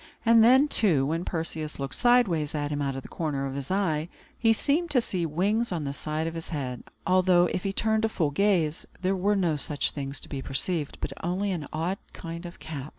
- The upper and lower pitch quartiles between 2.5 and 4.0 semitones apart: No, average, 5.0 semitones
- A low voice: No, medium, 165 Hz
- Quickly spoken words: Yes, fast, 225 wpm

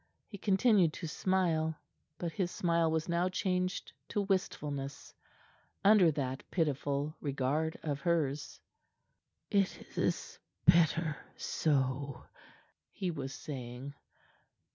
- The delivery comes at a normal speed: No, slow, 100 wpm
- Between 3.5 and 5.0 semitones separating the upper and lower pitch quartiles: Yes, average, 4.4 semitones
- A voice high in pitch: No, medium, 160 Hz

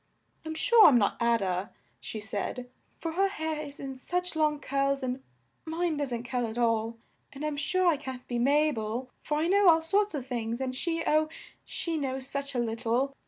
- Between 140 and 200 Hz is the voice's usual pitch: No, very high, 275 Hz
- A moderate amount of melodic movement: Yes, average, 4.8 semitones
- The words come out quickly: Yes, fast, 210 wpm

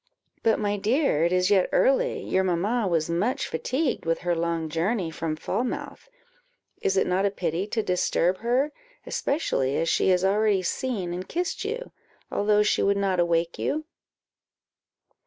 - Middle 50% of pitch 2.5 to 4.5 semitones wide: No, average, 5.3 semitones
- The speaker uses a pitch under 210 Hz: Yes, high, 190 Hz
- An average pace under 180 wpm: Yes, average, 160 wpm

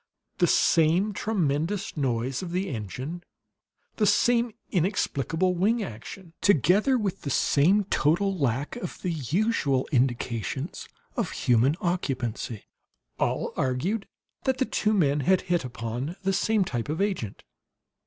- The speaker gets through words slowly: Yes, slow, 130 wpm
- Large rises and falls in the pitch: Yes, wide, 7.0 semitones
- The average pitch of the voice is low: No, medium, 170 Hz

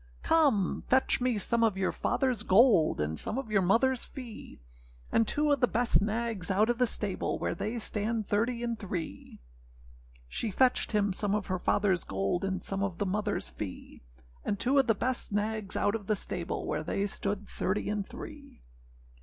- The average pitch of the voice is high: Yes, high, 210 Hz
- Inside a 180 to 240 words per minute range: Yes, average, 185 wpm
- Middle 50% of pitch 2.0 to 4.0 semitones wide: Yes, average, 3.4 semitones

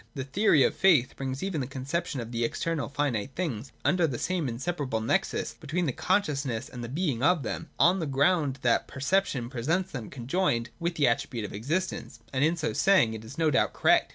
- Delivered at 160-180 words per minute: No, fast, 205 wpm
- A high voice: No, medium, 140 Hz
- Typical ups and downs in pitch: No, wide, 5.7 semitones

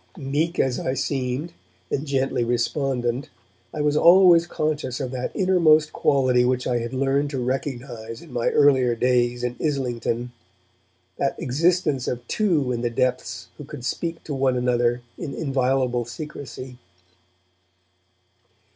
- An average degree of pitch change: Yes, average, 3.2 semitones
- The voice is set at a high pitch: No, low, 130 Hz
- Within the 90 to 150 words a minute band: Yes, average, 140 wpm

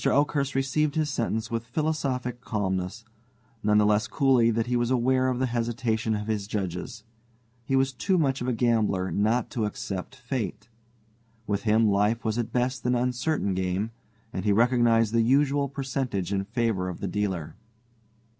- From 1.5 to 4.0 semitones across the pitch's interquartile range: Yes, average, 3.7 semitones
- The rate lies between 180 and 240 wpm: No, average, 170 wpm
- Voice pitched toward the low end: Yes, low, 115 Hz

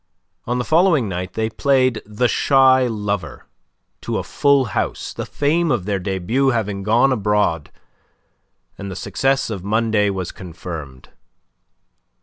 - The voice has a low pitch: Yes, low, 110 Hz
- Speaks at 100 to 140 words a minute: Yes, slow, 135 wpm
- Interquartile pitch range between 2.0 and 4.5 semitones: No, average, 5.3 semitones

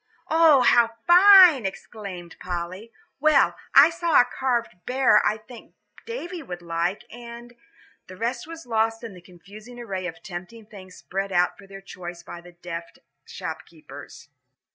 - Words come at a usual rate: Yes, average, 150 wpm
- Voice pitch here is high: Yes, high, 215 Hz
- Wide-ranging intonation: Yes, wide, 5.7 semitones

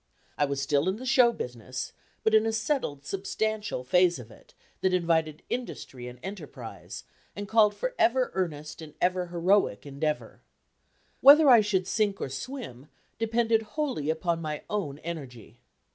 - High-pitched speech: No, medium, 180 Hz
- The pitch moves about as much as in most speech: No, wide, 7.2 semitones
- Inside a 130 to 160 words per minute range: Yes, average, 155 wpm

